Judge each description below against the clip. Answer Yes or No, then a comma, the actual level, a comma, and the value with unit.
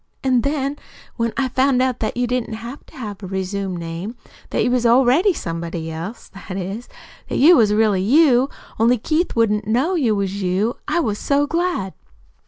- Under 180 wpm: No, average, 185 wpm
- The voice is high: Yes, high, 230 Hz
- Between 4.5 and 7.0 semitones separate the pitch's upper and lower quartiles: Yes, average, 5.1 semitones